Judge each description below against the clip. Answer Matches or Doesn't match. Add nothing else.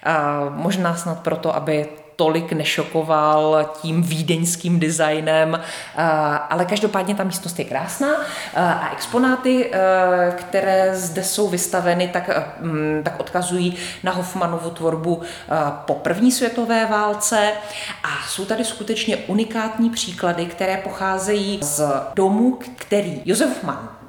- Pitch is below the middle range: Doesn't match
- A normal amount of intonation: Matches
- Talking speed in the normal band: Doesn't match